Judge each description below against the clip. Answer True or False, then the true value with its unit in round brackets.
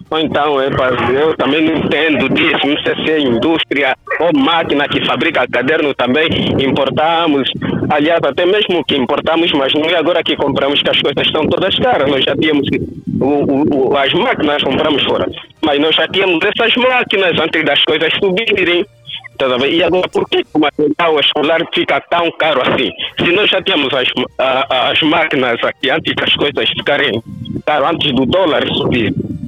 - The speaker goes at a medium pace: True (175 wpm)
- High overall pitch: False (160 Hz)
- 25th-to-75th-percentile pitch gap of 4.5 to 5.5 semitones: True (4.8 semitones)